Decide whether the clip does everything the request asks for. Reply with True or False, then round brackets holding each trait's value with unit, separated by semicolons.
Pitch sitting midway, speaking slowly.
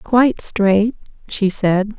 False (210 Hz; 120 wpm)